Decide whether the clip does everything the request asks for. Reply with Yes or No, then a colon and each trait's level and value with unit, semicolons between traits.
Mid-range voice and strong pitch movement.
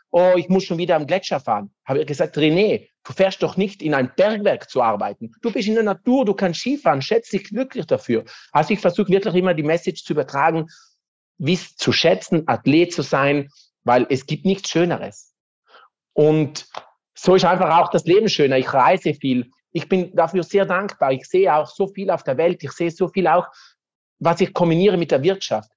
No: medium, 175 Hz; average, 4.2 semitones